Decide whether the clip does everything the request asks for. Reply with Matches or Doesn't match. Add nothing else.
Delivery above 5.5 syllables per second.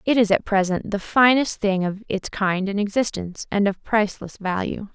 Doesn't match